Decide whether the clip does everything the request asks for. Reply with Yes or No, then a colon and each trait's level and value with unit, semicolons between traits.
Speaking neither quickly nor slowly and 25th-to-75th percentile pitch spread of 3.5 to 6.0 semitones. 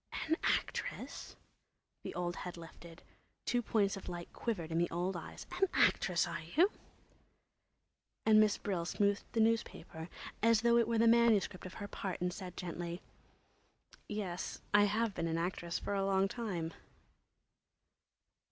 Yes: average, 150 wpm; average, 4.2 semitones